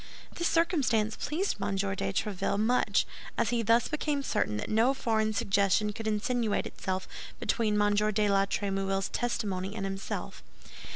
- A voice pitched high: Yes, high, 210 Hz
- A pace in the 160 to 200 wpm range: No, average, 150 wpm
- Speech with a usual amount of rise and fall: Yes, average, 3.1 semitones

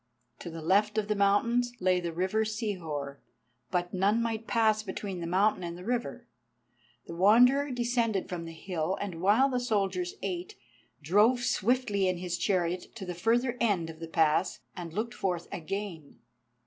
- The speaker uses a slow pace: No, average, 170 wpm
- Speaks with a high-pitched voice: Yes, high, 195 Hz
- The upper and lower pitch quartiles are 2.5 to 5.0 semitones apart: Yes, average, 4.3 semitones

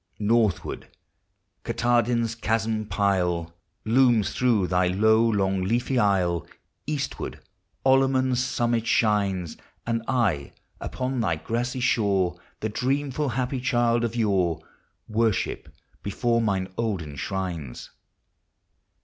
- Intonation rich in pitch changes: No, average, 4.1 semitones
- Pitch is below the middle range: Yes, low, 110 Hz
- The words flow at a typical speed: No, slow, 100 wpm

